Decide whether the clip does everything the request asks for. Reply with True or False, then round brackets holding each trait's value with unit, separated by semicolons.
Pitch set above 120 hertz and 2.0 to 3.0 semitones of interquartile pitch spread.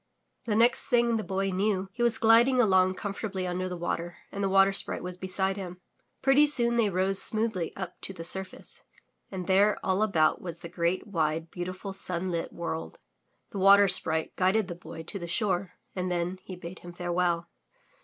True (185 Hz; 2.5 semitones)